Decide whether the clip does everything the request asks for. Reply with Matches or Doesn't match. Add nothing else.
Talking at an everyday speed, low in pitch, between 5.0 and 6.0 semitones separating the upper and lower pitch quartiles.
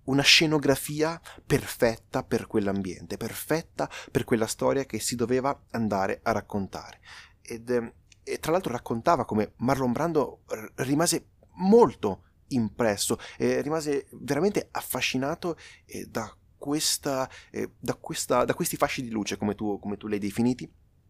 Matches